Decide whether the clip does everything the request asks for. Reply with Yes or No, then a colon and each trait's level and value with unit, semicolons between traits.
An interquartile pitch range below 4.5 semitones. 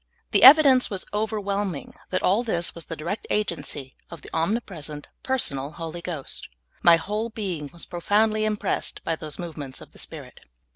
No: average, 5.0 semitones